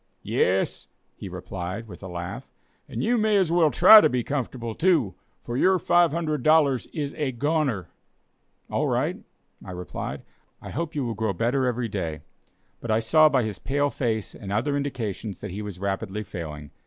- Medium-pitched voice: No, low, 120 Hz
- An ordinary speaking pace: Yes, average, 175 wpm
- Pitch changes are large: Yes, wide, 7.2 semitones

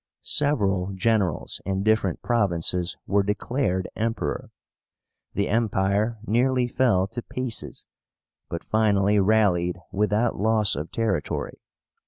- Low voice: Yes, low, 105 Hz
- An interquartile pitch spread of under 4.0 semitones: Yes, average, 3.0 semitones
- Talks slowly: Yes, slow, 105 wpm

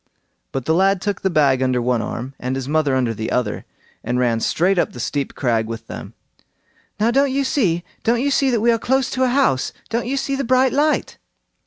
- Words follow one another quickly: Yes, fast, 225 wpm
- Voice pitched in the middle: Yes, medium, 175 Hz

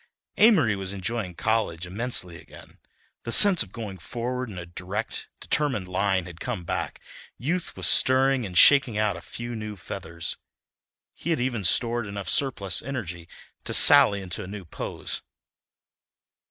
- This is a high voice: No, low, 105 Hz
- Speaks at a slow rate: No, average, 155 wpm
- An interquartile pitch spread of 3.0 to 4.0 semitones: No, average, 5.1 semitones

